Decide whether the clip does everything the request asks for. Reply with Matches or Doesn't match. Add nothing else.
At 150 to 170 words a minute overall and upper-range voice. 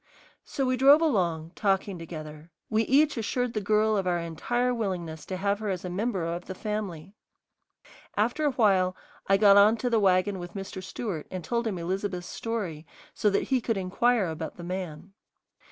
Doesn't match